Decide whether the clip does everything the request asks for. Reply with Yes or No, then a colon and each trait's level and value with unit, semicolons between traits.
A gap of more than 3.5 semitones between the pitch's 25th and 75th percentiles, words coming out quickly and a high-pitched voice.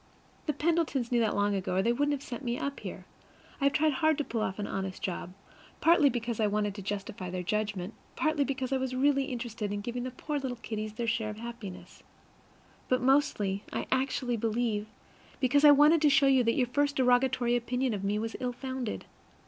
Yes: average, 4.4 semitones; fast, 215 wpm; high, 245 Hz